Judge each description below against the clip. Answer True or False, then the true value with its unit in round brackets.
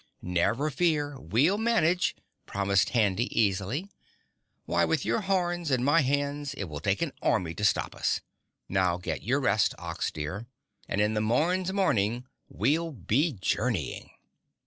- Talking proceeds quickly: False (145 wpm)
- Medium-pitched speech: False (125 Hz)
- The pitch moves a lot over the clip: True (8.0 semitones)